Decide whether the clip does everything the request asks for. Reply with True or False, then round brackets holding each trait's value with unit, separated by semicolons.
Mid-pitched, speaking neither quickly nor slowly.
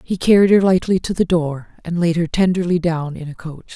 False (170 Hz; 240 wpm)